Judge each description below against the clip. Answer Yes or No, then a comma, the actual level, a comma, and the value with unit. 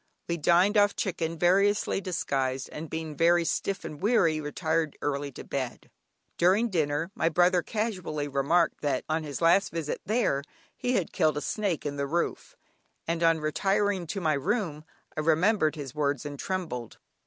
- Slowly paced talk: No, average, 165 wpm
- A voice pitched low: No, medium, 165 Hz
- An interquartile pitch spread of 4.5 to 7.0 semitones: No, average, 4.1 semitones